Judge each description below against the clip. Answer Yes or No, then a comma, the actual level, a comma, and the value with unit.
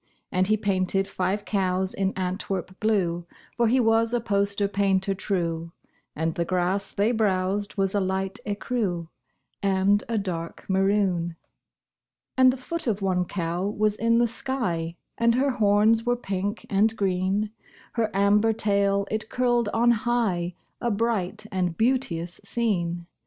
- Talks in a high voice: Yes, high, 200 Hz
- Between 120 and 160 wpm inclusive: Yes, average, 145 wpm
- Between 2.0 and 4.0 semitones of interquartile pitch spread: Yes, average, 3.2 semitones